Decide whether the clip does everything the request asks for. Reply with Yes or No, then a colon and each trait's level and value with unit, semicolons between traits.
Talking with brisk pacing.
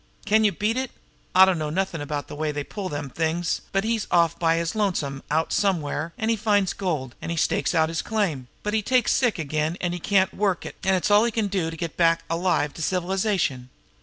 Yes: fast, 225 wpm